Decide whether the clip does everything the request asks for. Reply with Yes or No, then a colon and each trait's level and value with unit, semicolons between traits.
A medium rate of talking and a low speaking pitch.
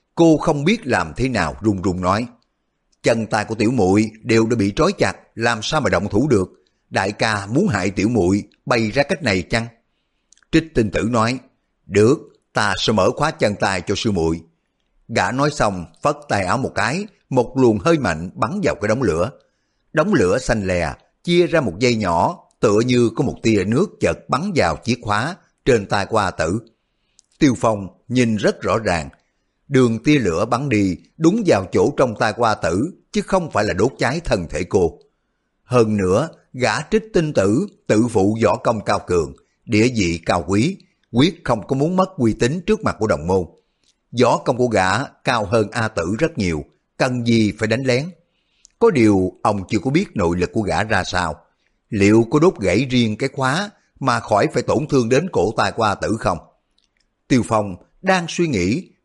Yes: average, 200 wpm; low, 115 Hz